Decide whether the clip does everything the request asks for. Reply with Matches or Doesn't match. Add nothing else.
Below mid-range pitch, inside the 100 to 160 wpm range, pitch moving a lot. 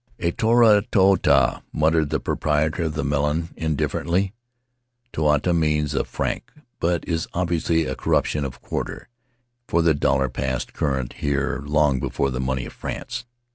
Doesn't match